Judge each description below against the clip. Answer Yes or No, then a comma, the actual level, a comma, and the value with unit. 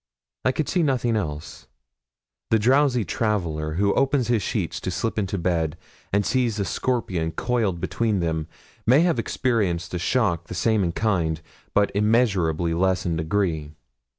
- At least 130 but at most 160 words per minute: Yes, average, 155 wpm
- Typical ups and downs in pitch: No, wide, 5.8 semitones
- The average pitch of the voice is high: No, low, 100 Hz